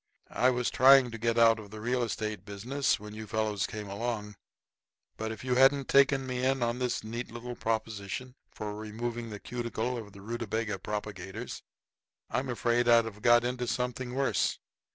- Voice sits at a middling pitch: No, low, 115 Hz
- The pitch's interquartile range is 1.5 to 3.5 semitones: Yes, narrow, 2.5 semitones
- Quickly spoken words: No, average, 175 wpm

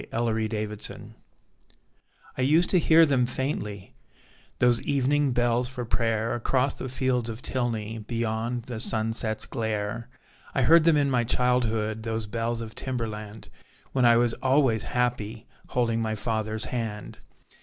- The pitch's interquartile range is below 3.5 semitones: Yes, narrow, 2.5 semitones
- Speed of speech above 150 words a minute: No, average, 140 wpm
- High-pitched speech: No, low, 115 Hz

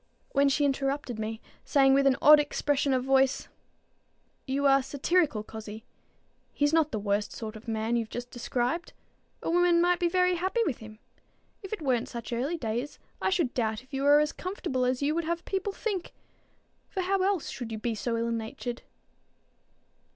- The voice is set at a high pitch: Yes, very high, 270 Hz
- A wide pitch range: Yes, wide, 6.1 semitones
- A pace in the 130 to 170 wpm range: No, average, 185 wpm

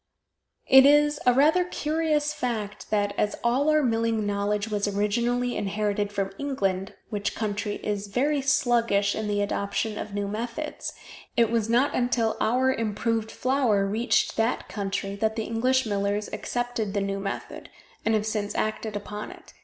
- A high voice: Yes, high, 220 Hz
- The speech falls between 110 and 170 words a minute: Yes, average, 160 wpm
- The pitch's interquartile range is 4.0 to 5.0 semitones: No, average, 3.3 semitones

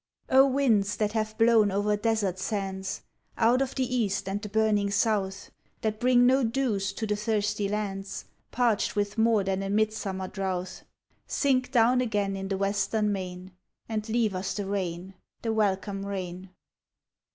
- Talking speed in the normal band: Yes, average, 155 wpm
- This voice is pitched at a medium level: No, high, 210 Hz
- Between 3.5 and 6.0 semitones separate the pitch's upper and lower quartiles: No, narrow, 2.5 semitones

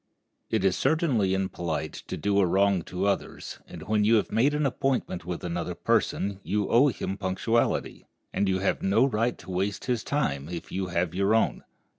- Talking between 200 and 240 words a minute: No, average, 190 wpm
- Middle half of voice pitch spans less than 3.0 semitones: No, average, 3.8 semitones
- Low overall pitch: Yes, low, 100 Hz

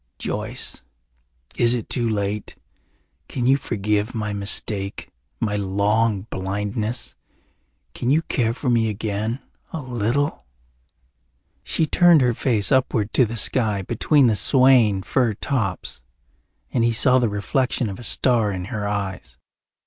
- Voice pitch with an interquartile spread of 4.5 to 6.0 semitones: No, average, 3.6 semitones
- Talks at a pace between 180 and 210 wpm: No, slow, 135 wpm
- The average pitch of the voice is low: Yes, low, 110 Hz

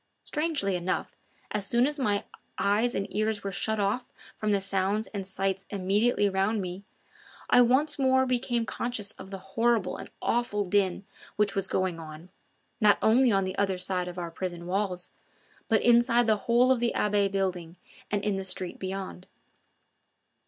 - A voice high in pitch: Yes, high, 200 Hz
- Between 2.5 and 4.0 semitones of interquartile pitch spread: Yes, average, 3.6 semitones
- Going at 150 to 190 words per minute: Yes, average, 170 wpm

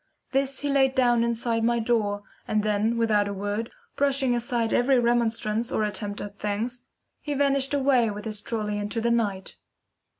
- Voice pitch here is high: Yes, high, 230 Hz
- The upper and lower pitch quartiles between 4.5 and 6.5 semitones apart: No, average, 3.0 semitones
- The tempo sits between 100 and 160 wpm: No, average, 170 wpm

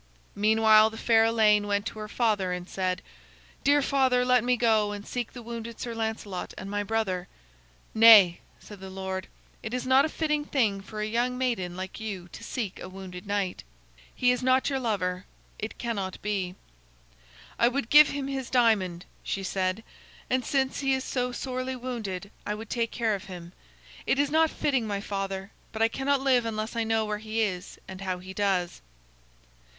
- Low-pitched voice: No, high, 220 Hz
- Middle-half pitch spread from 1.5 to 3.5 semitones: No, average, 4.3 semitones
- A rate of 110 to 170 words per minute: No, average, 190 wpm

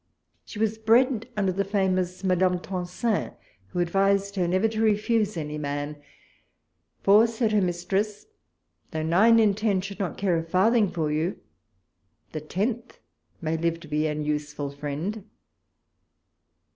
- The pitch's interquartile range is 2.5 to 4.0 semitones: No, average, 4.5 semitones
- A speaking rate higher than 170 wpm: No, average, 145 wpm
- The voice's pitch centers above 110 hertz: Yes, medium, 185 Hz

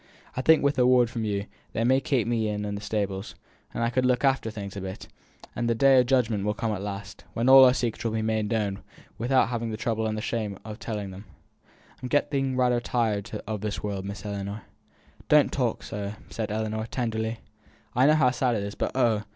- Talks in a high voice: No, low, 110 Hz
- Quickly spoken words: Yes, fast, 230 wpm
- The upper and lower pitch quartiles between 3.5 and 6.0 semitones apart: No, average, 3.1 semitones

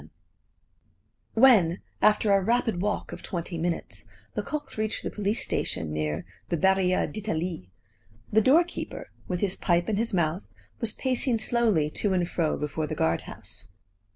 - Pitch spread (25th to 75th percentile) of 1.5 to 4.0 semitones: No, average, 4.8 semitones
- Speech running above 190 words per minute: No, average, 155 wpm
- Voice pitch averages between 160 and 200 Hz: Yes, high, 190 Hz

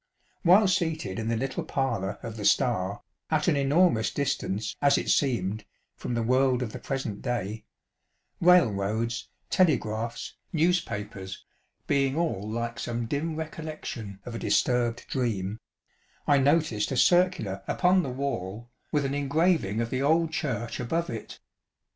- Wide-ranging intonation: Yes, wide, 5.8 semitones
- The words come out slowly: No, average, 150 wpm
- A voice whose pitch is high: No, low, 125 Hz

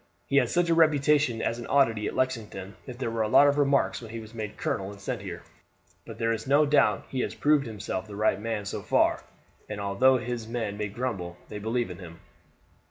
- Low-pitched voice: Yes, low, 115 Hz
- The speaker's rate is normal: No, fast, 235 wpm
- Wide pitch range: No, average, 4.0 semitones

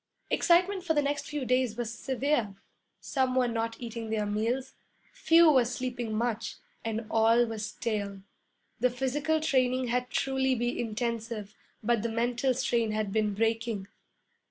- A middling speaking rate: Yes, average, 150 wpm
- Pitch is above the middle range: Yes, high, 240 Hz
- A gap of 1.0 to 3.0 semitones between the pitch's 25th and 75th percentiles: Yes, average, 2.7 semitones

